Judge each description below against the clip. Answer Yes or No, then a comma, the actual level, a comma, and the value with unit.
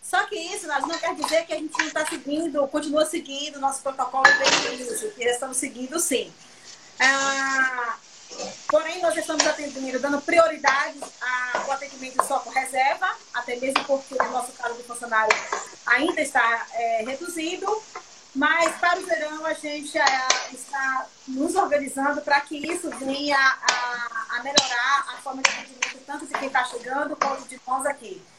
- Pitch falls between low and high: No, very high, 280 Hz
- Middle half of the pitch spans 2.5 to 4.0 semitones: Yes, average, 3.4 semitones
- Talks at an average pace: Yes, average, 165 wpm